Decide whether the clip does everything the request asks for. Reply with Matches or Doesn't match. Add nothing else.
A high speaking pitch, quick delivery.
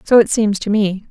Matches